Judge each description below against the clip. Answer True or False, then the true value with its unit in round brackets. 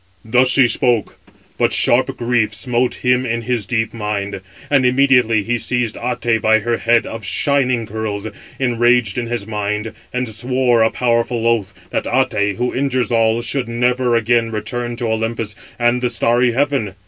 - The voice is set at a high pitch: False (120 Hz)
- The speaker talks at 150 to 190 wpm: True (165 wpm)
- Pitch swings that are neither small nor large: False (1.9 semitones)